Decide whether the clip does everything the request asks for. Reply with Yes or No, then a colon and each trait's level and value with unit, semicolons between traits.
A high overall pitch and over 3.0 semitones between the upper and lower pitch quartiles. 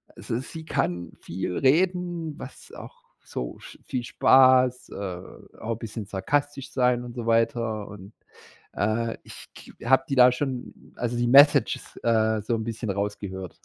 No: low, 115 Hz; average, 4.0 semitones